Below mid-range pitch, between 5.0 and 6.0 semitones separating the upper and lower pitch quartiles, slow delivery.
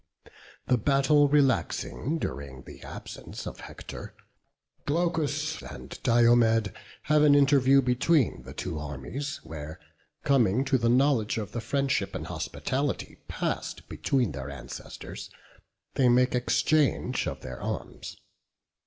Yes: low, 125 Hz; average, 5.3 semitones; slow, 120 wpm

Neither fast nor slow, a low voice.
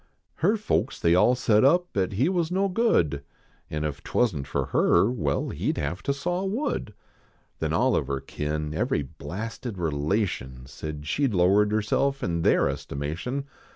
Yes: average, 175 wpm; low, 100 Hz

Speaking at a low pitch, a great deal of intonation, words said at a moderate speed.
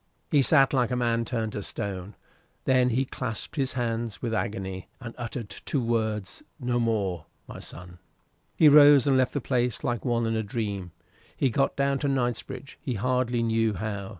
No: low, 120 Hz; average, 3.2 semitones; average, 180 wpm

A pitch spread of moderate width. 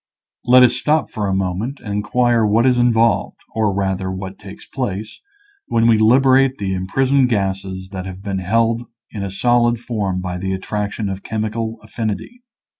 Yes: average, 3.8 semitones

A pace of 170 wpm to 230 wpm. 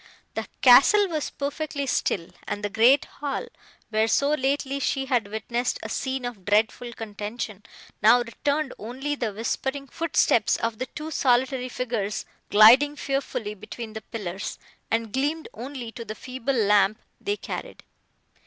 No: average, 145 wpm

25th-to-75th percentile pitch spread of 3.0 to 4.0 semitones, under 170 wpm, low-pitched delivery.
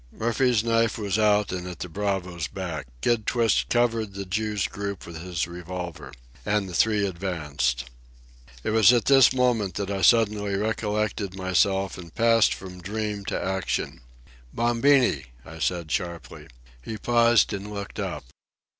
Yes: average, 3.6 semitones; average, 150 wpm; low, 100 Hz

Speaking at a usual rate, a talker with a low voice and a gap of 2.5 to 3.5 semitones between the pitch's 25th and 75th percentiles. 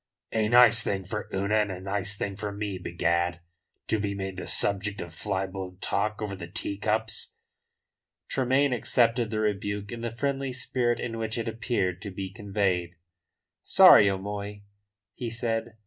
Yes: average, 165 wpm; low, 105 Hz; average, 2.8 semitones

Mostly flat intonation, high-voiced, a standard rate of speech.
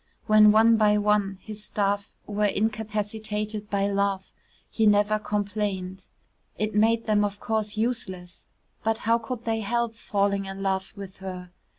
Yes: narrow, 1.7 semitones; high, 210 Hz; average, 150 wpm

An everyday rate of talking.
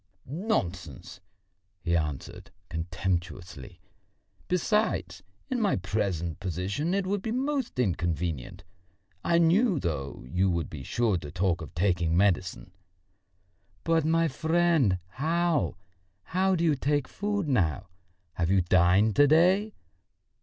No: slow, 120 wpm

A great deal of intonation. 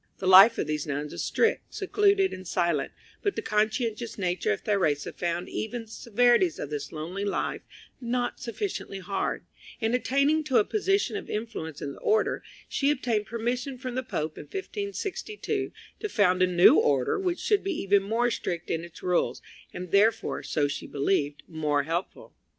Yes: wide, 6.8 semitones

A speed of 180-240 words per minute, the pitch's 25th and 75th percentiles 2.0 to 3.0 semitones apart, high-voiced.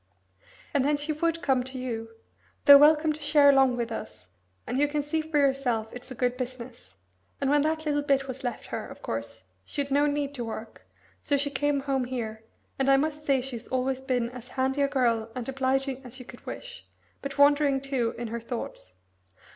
Yes: fast, 205 wpm; narrow, 2.6 semitones; very high, 270 Hz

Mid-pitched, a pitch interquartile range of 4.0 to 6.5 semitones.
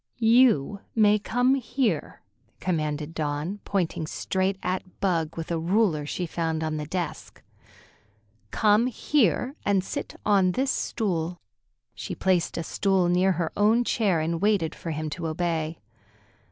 Yes: medium, 180 Hz; average, 4.3 semitones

